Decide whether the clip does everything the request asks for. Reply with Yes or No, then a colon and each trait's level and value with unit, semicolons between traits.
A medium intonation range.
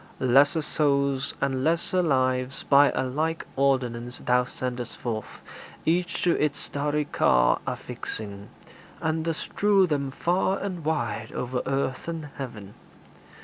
Yes: average, 4.1 semitones